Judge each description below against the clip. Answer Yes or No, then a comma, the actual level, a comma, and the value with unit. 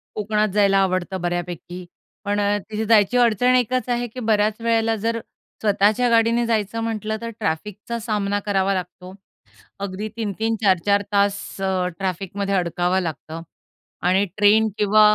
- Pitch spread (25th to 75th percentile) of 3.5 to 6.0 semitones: No, average, 2.7 semitones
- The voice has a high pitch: Yes, high, 205 Hz